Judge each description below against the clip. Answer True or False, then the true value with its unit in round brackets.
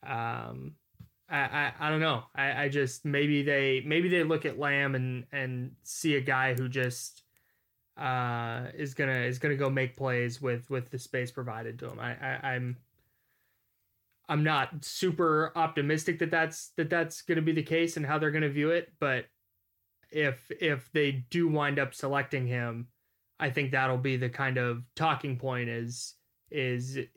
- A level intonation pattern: False (3.4 semitones)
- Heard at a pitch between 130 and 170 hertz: True (135 Hz)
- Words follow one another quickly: False (175 wpm)